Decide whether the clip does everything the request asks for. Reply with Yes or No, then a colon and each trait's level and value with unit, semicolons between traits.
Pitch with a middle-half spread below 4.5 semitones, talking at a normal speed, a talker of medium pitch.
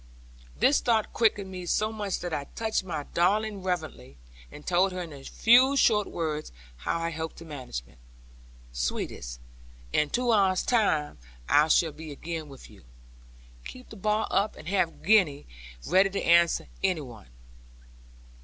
No: wide, 5.5 semitones; average, 160 wpm; medium, 175 Hz